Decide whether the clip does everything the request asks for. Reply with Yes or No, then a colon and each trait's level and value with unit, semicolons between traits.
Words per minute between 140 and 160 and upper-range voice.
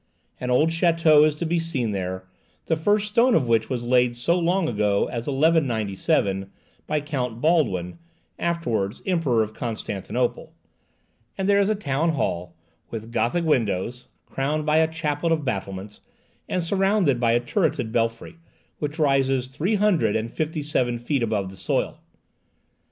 No: average, 155 wpm; low, 135 Hz